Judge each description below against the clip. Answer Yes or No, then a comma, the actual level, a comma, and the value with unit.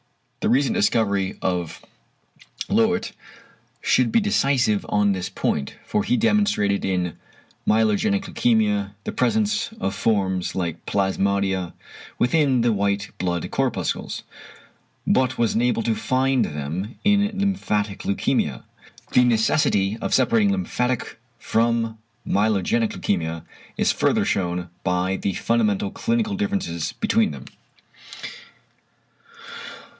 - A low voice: Yes, low, 110 Hz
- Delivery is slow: Yes, slow, 110 wpm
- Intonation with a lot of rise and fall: Yes, wide, 7.7 semitones